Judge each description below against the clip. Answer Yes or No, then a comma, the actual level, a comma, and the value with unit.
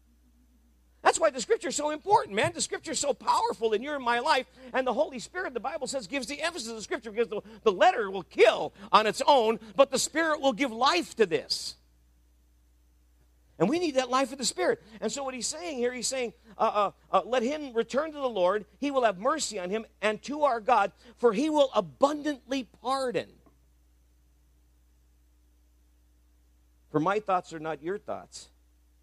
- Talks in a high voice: Yes, high, 230 Hz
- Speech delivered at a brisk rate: No, average, 195 wpm